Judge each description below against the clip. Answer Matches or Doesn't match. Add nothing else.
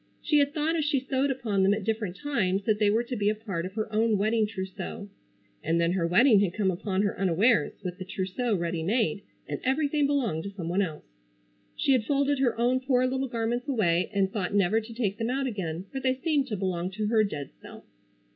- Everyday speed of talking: Doesn't match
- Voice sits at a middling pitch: Doesn't match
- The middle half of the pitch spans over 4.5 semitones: Matches